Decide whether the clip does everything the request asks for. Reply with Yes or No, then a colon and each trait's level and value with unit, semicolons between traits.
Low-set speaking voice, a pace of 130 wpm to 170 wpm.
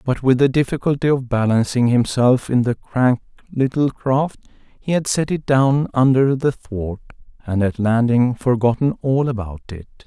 Yes: low, 125 Hz; average, 160 wpm